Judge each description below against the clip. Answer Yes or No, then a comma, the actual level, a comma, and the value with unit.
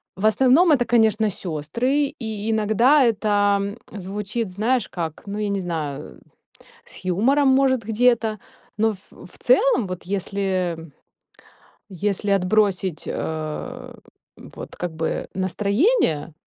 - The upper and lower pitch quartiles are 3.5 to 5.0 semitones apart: Yes, average, 4.2 semitones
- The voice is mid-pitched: No, high, 205 Hz